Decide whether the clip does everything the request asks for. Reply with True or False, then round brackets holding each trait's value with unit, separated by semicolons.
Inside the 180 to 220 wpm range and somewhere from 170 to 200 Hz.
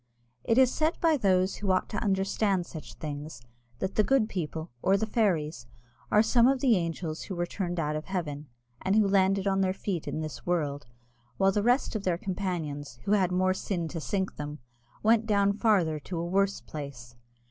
True (200 wpm; 185 Hz)